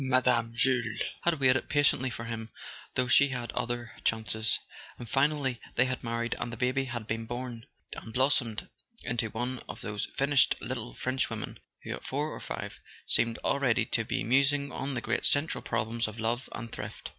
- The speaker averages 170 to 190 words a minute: Yes, average, 180 wpm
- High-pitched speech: No, low, 120 Hz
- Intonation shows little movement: Yes, narrow, 2.3 semitones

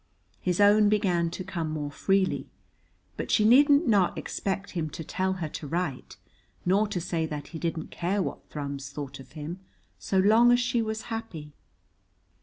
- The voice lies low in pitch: No, medium, 180 Hz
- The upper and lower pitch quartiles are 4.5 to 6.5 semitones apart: Yes, average, 5.0 semitones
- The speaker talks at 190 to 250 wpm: No, average, 175 wpm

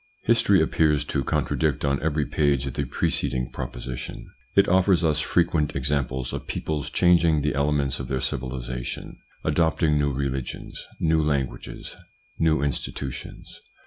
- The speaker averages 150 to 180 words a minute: No, slow, 135 wpm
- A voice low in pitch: Yes, very low, 70 Hz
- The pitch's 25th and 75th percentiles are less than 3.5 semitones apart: Yes, average, 2.9 semitones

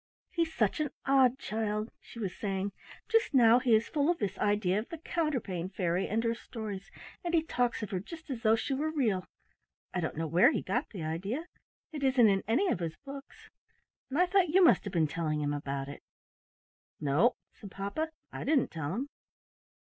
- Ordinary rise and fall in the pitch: No, wide, 7.1 semitones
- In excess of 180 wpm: Yes, average, 200 wpm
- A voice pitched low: No, high, 225 Hz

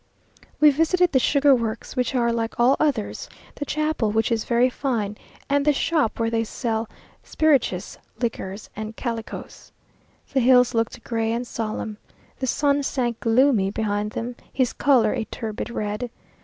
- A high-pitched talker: Yes, high, 235 Hz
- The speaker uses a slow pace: No, average, 155 wpm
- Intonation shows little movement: No, average, 3.5 semitones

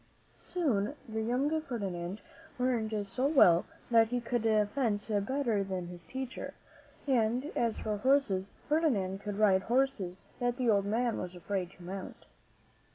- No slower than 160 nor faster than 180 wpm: No, average, 150 wpm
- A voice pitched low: No, high, 220 Hz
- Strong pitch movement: No, average, 4.5 semitones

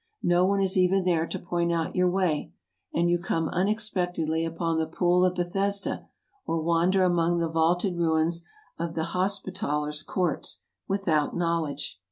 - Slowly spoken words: No, average, 170 wpm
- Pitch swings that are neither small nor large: No, narrow, 1.9 semitones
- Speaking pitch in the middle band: Yes, medium, 175 Hz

